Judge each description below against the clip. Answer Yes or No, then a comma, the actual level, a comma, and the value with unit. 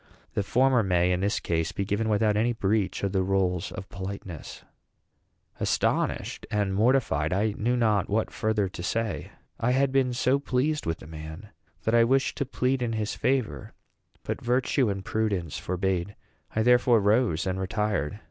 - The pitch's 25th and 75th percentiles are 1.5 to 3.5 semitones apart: No, average, 4.2 semitones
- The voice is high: No, low, 105 Hz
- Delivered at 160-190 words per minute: Yes, average, 170 wpm